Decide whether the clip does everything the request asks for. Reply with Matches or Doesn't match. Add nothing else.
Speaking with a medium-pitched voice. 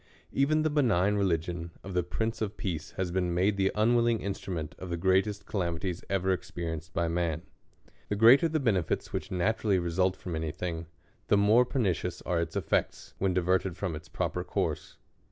Doesn't match